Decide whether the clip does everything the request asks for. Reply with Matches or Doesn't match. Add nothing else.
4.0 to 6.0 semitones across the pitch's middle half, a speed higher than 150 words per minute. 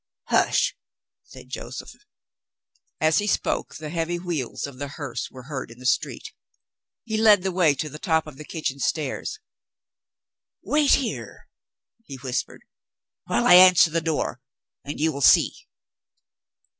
Doesn't match